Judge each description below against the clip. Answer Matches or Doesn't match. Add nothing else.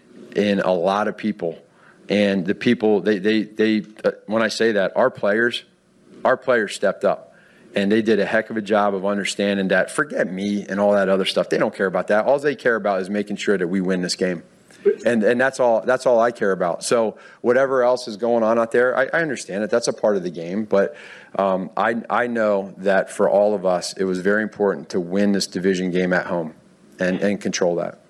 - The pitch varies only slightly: Matches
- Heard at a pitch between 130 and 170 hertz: Doesn't match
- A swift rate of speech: Matches